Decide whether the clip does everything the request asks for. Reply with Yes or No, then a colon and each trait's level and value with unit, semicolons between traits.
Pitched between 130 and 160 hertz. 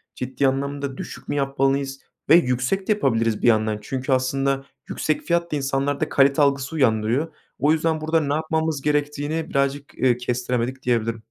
Yes: medium, 140 Hz